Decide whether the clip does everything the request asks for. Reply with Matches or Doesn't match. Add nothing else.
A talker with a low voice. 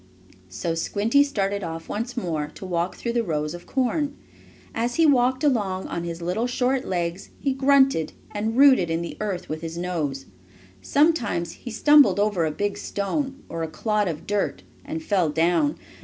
Doesn't match